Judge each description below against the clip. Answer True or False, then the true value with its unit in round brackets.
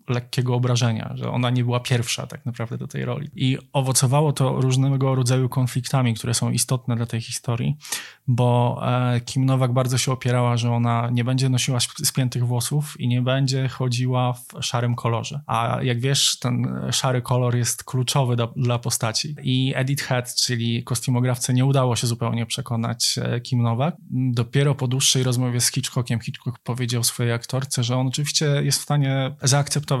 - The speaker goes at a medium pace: False (170 wpm)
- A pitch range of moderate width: False (1.7 semitones)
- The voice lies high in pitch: False (125 Hz)